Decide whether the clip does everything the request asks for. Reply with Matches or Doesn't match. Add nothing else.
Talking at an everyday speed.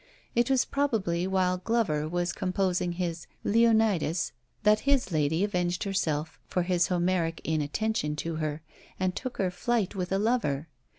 Matches